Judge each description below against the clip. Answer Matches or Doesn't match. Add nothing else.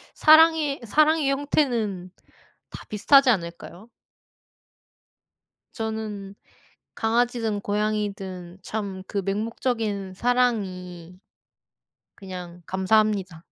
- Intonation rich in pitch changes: Doesn't match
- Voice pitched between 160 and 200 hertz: Doesn't match